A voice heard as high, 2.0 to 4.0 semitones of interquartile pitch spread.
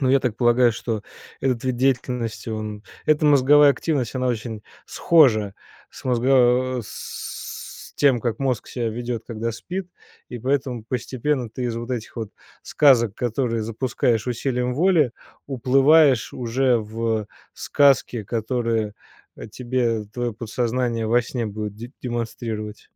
No: low, 120 Hz; narrow, 2.4 semitones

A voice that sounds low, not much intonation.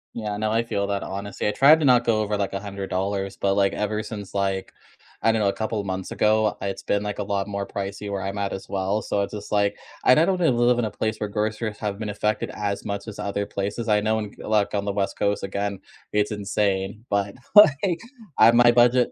Yes: low, 105 Hz; narrow, 1.6 semitones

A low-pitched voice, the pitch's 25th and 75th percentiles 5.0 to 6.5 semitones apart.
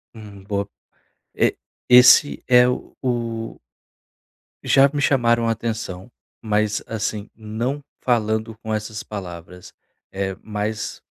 No: low, 110 Hz; narrow, 2.4 semitones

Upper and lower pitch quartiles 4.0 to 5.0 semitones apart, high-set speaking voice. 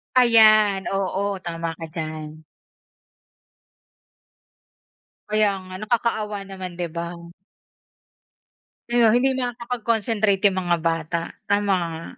Yes: average, 4.5 semitones; high, 195 Hz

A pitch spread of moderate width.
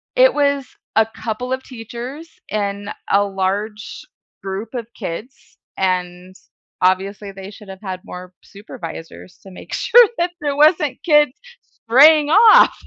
No: wide, 6.8 semitones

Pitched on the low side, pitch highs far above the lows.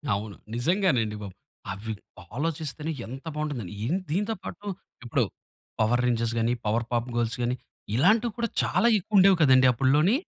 Yes: low, 130 Hz; wide, 6.8 semitones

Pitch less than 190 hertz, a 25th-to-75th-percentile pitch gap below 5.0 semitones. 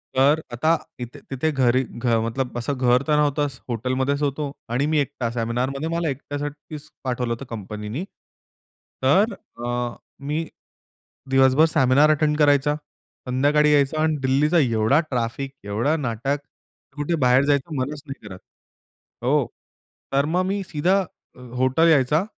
Yes: medium, 140 Hz; average, 3.3 semitones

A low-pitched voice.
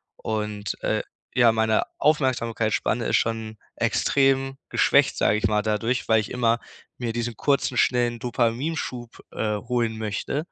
Yes: low, 115 Hz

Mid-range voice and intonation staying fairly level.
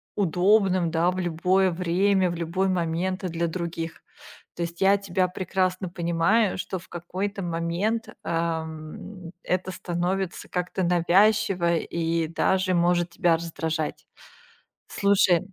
Yes: medium, 175 Hz; narrow, 2.1 semitones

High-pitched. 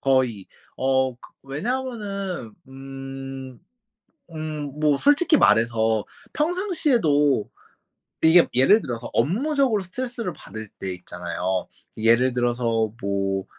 No: low, 135 Hz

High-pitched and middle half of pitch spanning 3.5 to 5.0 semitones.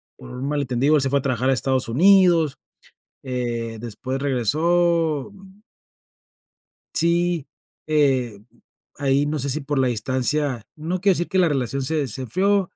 No: medium, 140 Hz; average, 4.5 semitones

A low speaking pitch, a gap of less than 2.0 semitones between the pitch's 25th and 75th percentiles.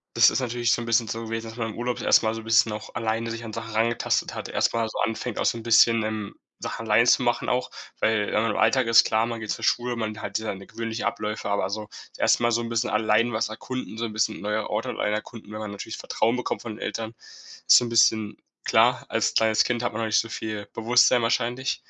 Yes: low, 115 Hz; narrow, 1.3 semitones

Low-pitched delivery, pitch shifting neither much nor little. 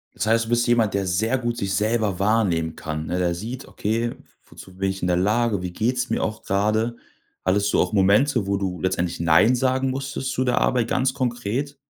Yes: low, 110 Hz; average, 4.2 semitones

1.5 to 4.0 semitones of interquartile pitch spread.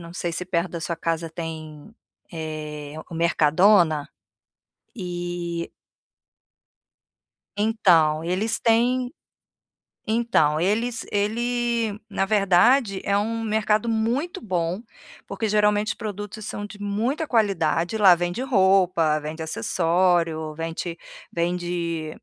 No: average, 4.7 semitones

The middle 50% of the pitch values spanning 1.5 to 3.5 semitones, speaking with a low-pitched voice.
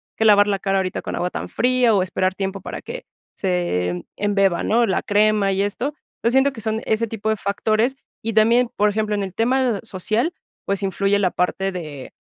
No: average, 2.8 semitones; high, 205 Hz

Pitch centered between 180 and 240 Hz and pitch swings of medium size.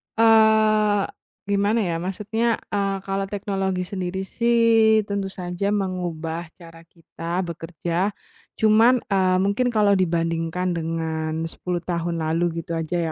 Yes: medium, 185 Hz; average, 3.7 semitones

